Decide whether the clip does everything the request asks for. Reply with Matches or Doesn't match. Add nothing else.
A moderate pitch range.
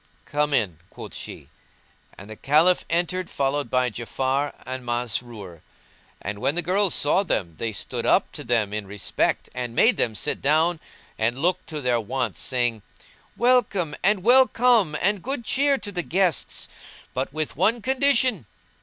Doesn't match